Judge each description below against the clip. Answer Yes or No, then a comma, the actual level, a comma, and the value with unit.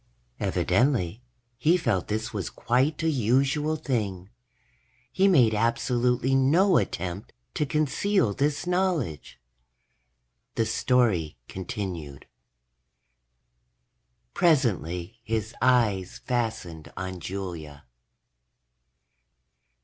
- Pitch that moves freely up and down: Yes, wide, 6.7 semitones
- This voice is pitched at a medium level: No, low, 115 Hz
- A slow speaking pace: Yes, slow, 85 wpm